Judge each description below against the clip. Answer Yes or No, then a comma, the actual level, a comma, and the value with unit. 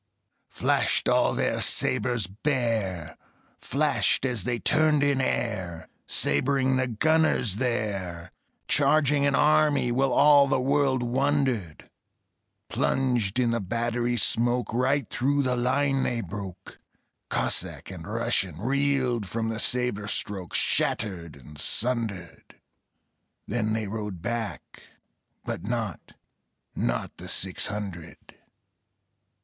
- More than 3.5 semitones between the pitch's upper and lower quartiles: Yes, average, 4.8 semitones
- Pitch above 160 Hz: No, low, 120 Hz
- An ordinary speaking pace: No, slow, 110 wpm